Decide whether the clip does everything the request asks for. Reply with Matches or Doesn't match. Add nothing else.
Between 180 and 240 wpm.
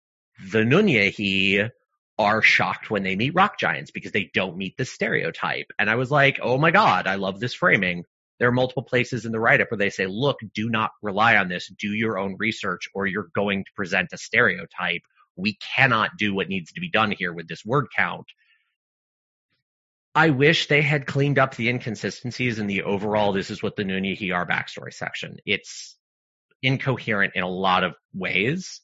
Matches